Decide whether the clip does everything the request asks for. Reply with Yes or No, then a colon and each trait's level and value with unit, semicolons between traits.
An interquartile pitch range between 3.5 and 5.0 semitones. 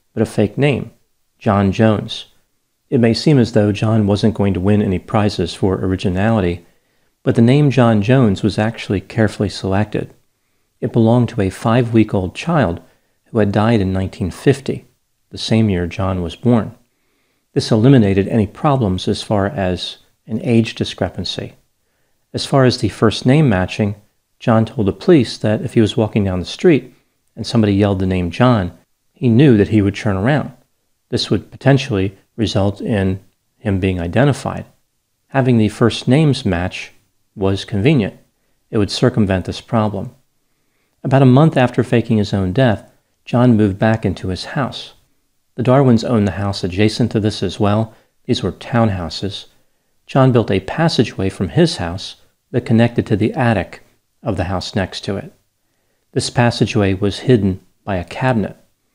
Yes: average, 3.9 semitones